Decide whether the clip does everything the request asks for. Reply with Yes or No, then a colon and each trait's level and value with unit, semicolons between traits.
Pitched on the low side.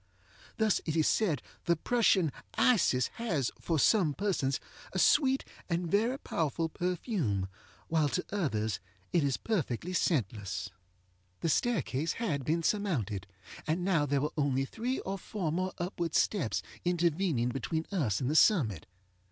No: medium, 165 Hz